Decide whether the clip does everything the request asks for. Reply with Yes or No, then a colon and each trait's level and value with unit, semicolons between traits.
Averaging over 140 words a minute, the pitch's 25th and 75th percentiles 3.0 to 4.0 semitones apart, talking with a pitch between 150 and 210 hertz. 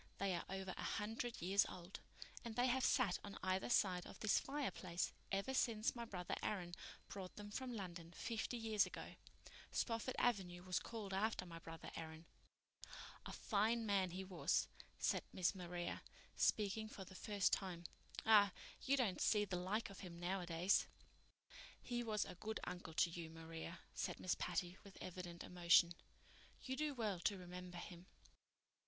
Yes: average, 165 wpm; average, 3.7 semitones; high, 190 Hz